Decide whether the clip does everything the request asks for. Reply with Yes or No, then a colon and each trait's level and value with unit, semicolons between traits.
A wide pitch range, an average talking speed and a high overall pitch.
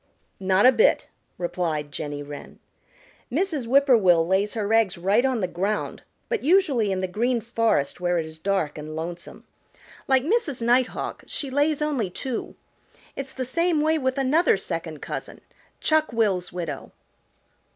Yes: wide, 7.4 semitones; average, 160 wpm; high, 225 Hz